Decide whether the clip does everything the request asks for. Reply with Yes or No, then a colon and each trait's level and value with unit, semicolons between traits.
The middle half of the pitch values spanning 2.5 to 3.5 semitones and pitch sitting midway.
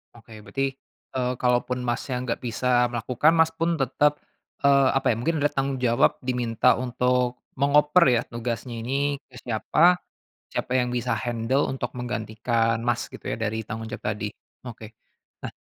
No: average, 2.8 semitones; low, 125 Hz